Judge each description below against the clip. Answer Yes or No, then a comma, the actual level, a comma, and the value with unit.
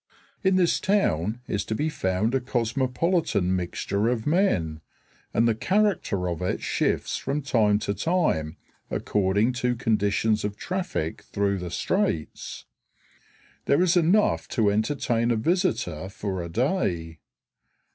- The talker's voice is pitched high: No, low, 110 Hz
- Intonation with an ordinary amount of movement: No, wide, 7.9 semitones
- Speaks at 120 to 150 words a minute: Yes, slow, 135 wpm